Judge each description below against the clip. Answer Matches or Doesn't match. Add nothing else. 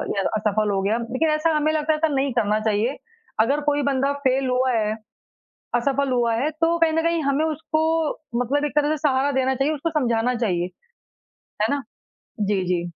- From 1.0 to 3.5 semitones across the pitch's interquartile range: Doesn't match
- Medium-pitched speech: Doesn't match